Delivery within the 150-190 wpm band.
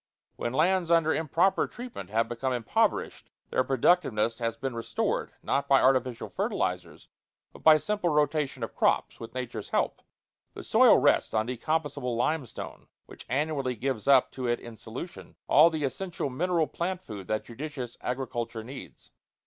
Yes: average, 155 wpm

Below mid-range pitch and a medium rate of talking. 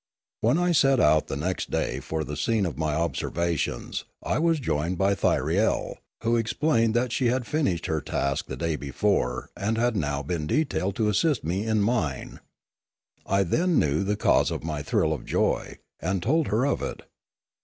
Yes: very low, 95 Hz; average, 180 wpm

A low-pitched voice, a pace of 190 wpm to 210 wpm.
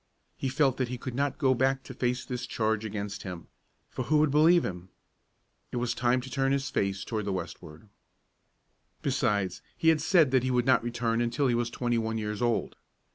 Yes: low, 120 Hz; fast, 205 wpm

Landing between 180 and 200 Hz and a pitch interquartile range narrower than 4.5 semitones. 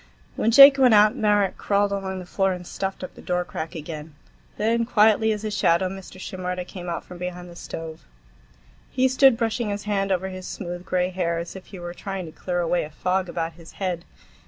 Yes: medium, 185 Hz; average, 2.8 semitones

